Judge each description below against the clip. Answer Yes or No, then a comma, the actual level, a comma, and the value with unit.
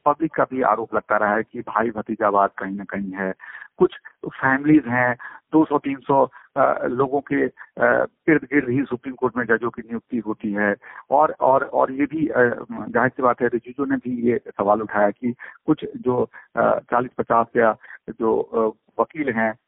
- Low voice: Yes, low, 120 Hz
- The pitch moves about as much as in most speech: Yes, average, 4.2 semitones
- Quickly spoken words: No, average, 170 wpm